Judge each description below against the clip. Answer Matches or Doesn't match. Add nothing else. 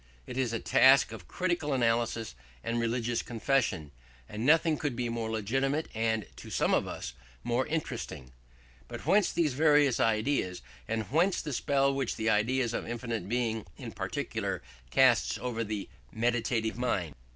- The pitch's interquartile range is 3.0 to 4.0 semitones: Matches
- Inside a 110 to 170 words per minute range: Matches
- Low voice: Matches